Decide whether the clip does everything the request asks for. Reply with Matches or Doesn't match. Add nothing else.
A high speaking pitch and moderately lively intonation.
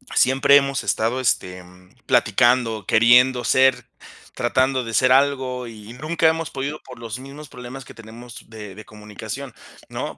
Doesn't match